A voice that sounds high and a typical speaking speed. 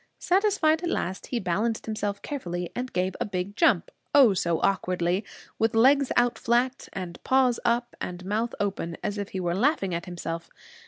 Yes: high, 205 Hz; average, 175 wpm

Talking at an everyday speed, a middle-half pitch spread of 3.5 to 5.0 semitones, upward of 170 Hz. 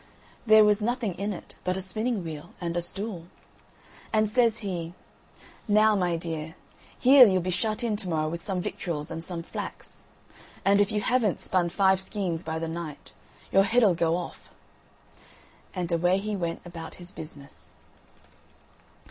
Yes: average, 165 wpm; average, 3.9 semitones; medium, 185 Hz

